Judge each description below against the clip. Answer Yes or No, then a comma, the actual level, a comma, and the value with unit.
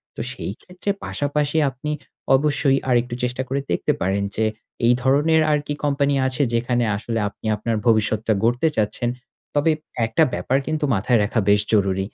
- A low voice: Yes, low, 125 Hz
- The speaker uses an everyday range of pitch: Yes, average, 4.5 semitones